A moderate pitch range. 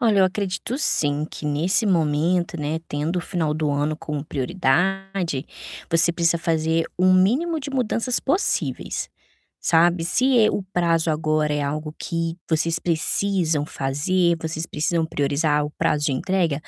Yes: average, 3.6 semitones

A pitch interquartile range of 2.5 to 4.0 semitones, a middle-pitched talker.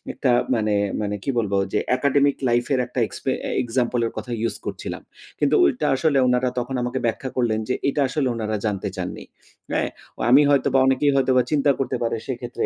No: average, 2.8 semitones; low, 125 Hz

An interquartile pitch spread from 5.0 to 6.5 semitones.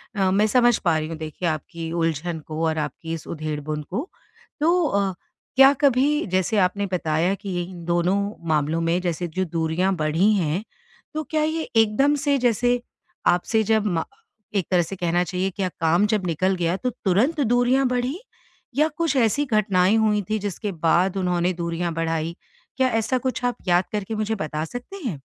Yes: average, 5.3 semitones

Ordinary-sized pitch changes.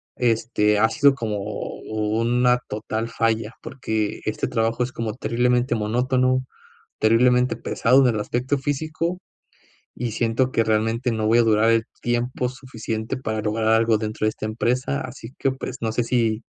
No: narrow, 2.3 semitones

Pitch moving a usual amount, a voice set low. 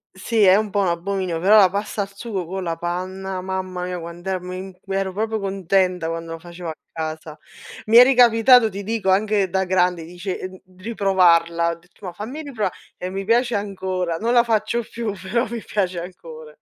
No: average, 3.1 semitones; high, 190 Hz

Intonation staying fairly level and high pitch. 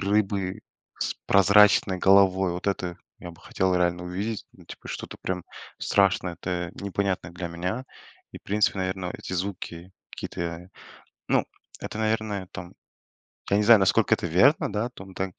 No: narrow, 2.2 semitones; very low, 95 Hz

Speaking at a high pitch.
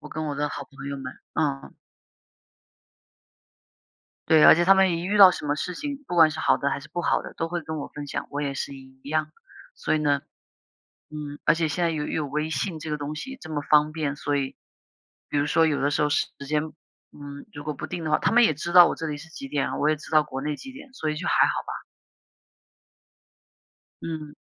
No: medium, 150 Hz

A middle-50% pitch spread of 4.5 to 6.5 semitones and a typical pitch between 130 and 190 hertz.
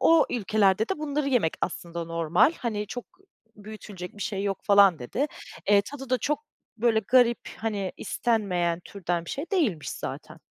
No: average, 5.3 semitones; high, 210 Hz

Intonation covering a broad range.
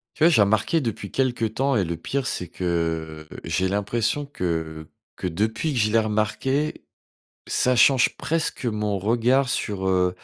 Yes: wide, 5.9 semitones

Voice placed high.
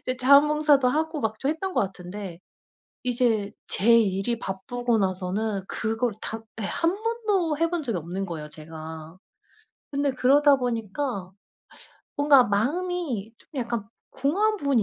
Yes: high, 240 Hz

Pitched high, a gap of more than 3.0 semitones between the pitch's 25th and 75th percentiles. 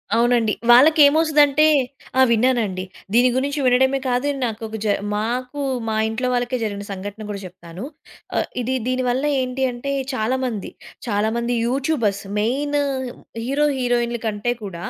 Yes: high, 245 Hz; average, 3.4 semitones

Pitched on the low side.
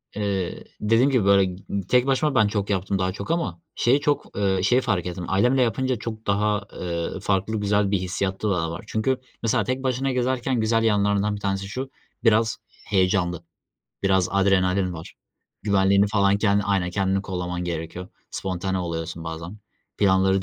Yes: low, 100 Hz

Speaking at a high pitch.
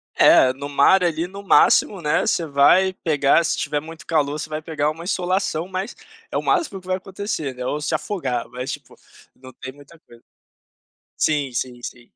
No: medium, 155 Hz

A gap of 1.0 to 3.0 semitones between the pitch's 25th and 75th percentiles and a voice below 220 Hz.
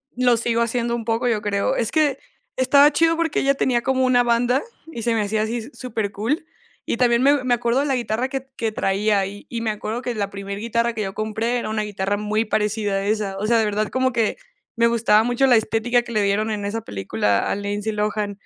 No: average, 2.7 semitones; high, 225 Hz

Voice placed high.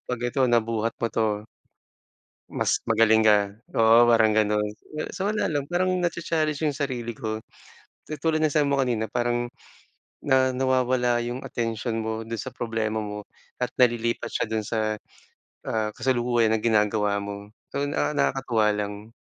No: low, 115 Hz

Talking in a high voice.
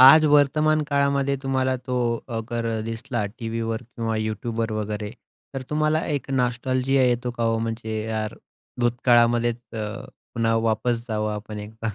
No: low, 120 Hz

